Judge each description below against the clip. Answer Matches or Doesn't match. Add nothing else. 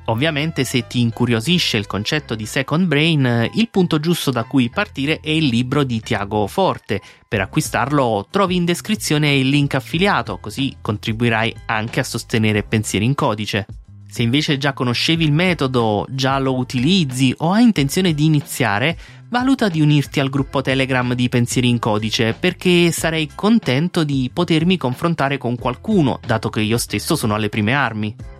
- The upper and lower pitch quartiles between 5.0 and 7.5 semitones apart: Matches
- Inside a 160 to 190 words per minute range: Matches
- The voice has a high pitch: Doesn't match